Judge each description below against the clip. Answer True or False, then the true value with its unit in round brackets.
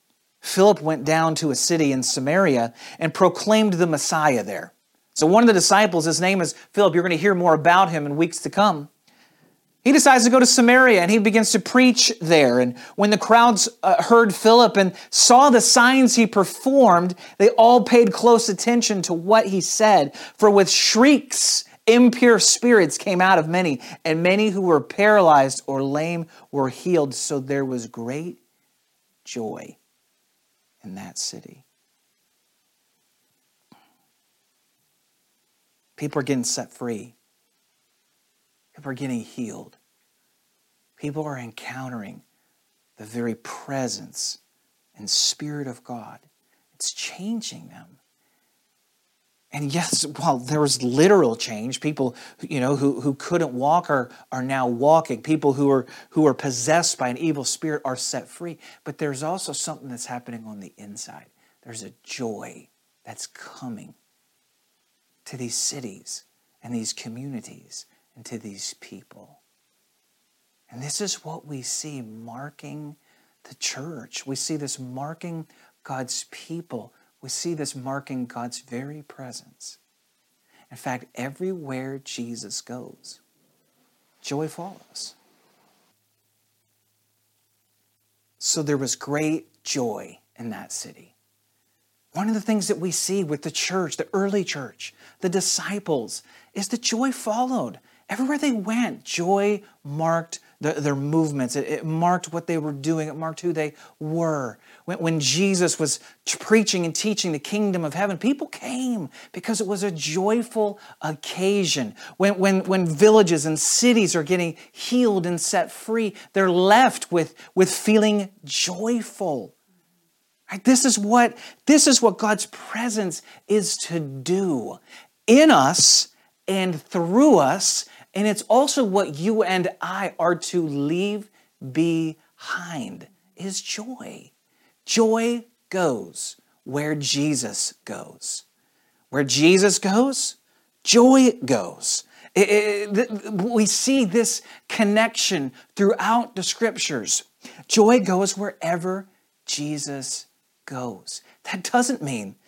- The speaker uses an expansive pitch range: True (6.9 semitones)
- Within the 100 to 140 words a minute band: True (135 wpm)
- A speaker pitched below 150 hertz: False (175 Hz)